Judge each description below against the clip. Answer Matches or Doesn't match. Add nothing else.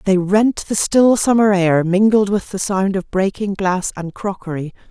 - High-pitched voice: Matches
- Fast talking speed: Doesn't match